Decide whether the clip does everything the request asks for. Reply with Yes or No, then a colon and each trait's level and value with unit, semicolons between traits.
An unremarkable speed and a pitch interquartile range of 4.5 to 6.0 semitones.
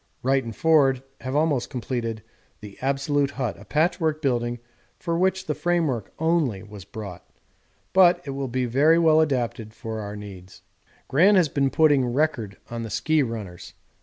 Yes: average, 165 wpm; wide, 5.5 semitones